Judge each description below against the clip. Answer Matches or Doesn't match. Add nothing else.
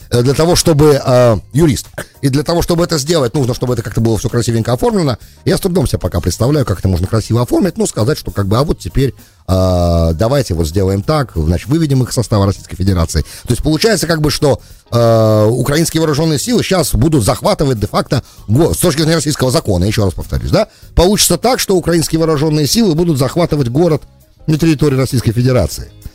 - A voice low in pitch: Matches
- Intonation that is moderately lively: Doesn't match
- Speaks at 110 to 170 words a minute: Doesn't match